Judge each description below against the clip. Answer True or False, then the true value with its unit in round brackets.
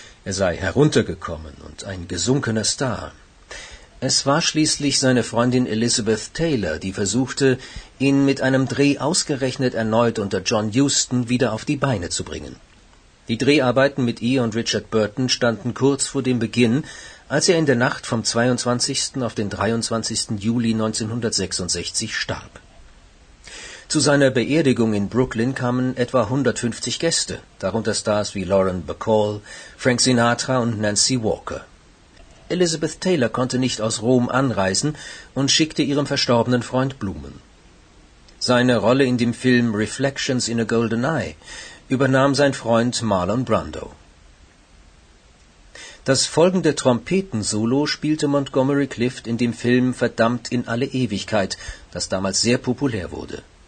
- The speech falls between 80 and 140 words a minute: True (135 wpm)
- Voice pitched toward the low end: True (120 Hz)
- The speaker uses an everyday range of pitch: True (3.7 semitones)